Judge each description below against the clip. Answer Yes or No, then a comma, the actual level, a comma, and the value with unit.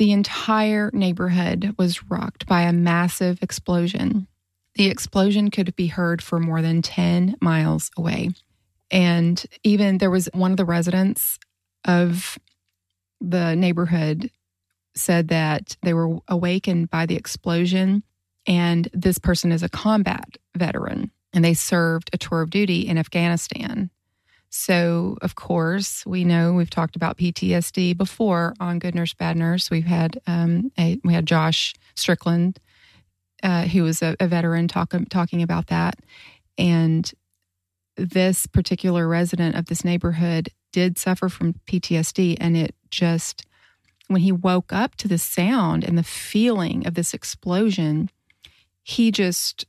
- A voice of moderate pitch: Yes, medium, 175 Hz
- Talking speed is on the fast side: No, average, 140 wpm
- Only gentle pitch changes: Yes, narrow, 2.0 semitones